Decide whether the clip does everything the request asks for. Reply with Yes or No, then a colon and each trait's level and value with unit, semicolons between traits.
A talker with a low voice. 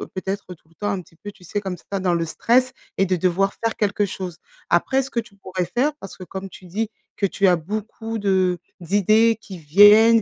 No: high, 195 Hz